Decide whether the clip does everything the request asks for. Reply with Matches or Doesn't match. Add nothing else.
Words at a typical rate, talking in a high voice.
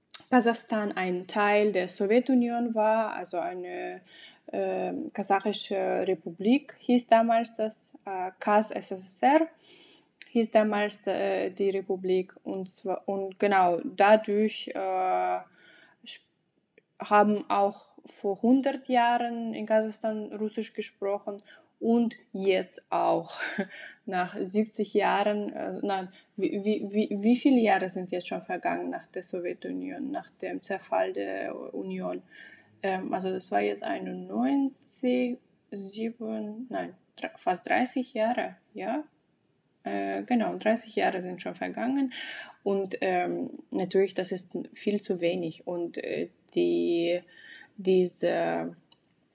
Doesn't match